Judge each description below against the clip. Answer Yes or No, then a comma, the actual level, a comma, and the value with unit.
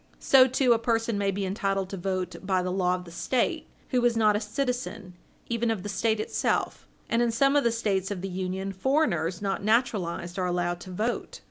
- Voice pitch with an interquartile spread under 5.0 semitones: Yes, average, 4.0 semitones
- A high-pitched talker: Yes, high, 205 Hz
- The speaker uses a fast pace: Yes, fast, 215 wpm